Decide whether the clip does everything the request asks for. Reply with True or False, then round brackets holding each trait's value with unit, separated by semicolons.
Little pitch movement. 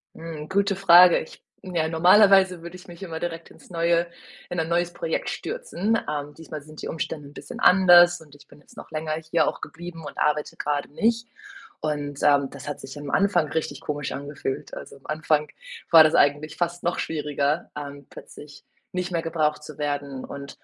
False (3.0 semitones)